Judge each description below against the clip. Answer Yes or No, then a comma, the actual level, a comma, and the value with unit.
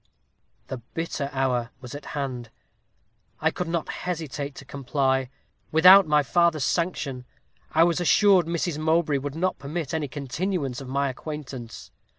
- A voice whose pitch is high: No, medium, 145 Hz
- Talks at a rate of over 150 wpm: No, average, 145 wpm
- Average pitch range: Yes, average, 3.9 semitones